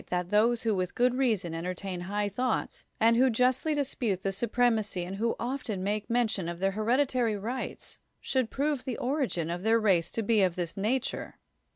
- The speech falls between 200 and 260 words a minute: Yes, fast, 205 wpm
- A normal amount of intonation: Yes, average, 4.5 semitones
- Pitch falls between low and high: No, high, 220 Hz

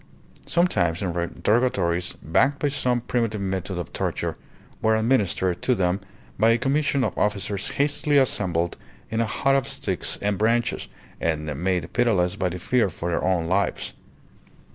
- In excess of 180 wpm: No, average, 150 wpm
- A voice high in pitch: No, low, 105 Hz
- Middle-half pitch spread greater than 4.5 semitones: Yes, wide, 5.5 semitones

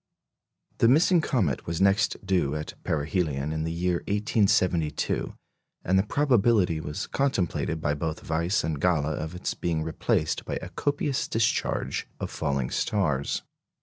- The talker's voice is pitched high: No, very low, 85 Hz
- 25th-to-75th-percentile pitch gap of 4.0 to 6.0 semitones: Yes, average, 5.0 semitones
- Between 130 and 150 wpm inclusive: Yes, average, 145 wpm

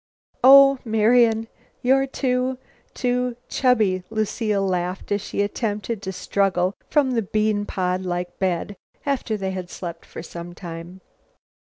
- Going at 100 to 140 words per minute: Yes, slow, 135 wpm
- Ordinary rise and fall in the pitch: Yes, average, 5.0 semitones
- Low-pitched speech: No, high, 205 Hz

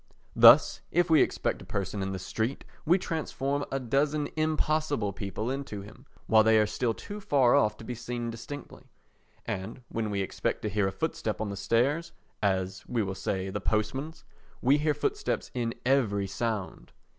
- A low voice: Yes, low, 115 Hz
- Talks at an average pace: Yes, average, 170 wpm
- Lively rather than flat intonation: Yes, wide, 5.7 semitones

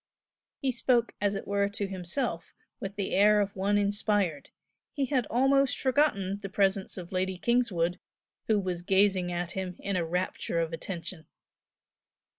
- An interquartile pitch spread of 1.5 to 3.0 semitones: Yes, average, 2.7 semitones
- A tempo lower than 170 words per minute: Yes, average, 155 wpm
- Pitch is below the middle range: No, high, 195 Hz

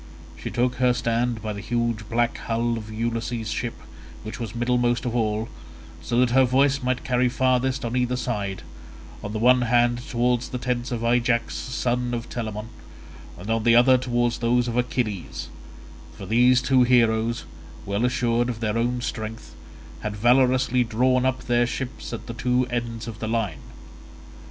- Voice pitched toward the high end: No, low, 120 Hz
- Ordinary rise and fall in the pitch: No, narrow, 1.4 semitones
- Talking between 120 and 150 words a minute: No, average, 170 wpm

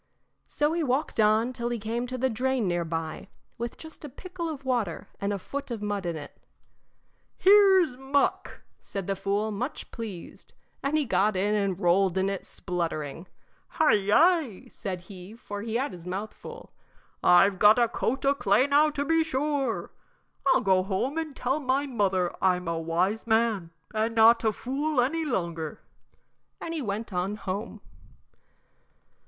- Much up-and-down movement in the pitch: Yes, wide, 6.1 semitones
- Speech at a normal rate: Yes, average, 170 wpm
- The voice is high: Yes, high, 220 Hz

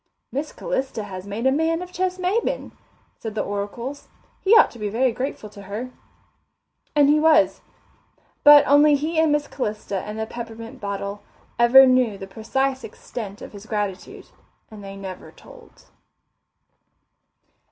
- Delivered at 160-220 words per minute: No, average, 150 wpm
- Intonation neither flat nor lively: No, wide, 6.0 semitones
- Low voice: No, high, 235 Hz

